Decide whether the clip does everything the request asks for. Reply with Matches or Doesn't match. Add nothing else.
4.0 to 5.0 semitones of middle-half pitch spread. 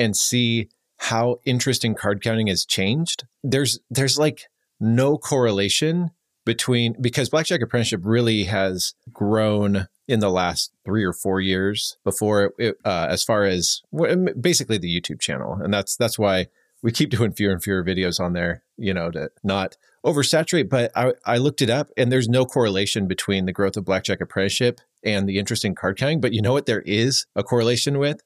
Matches